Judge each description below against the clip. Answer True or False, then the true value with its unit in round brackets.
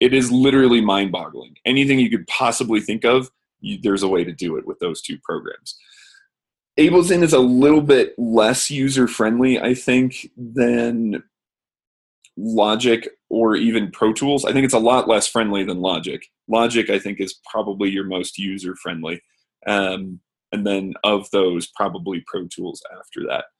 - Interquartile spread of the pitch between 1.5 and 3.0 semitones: False (5.0 semitones)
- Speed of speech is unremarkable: True (170 wpm)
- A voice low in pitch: True (115 Hz)